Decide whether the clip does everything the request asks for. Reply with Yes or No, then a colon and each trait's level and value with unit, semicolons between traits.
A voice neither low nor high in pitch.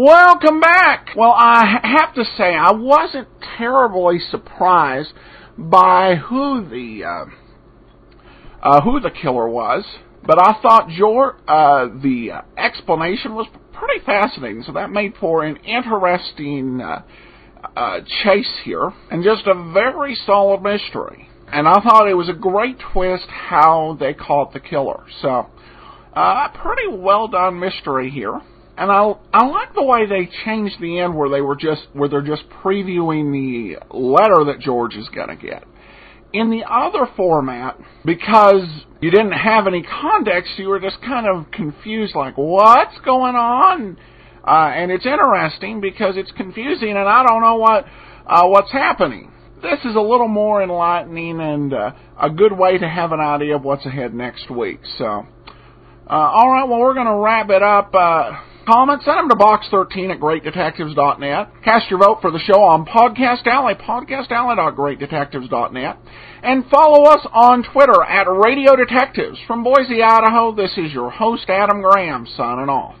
No: high, 200 Hz